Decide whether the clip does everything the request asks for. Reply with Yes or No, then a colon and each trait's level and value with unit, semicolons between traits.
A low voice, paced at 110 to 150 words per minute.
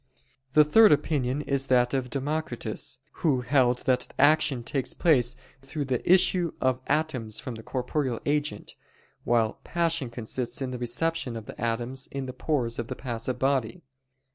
No: low, 130 Hz; average, 160 wpm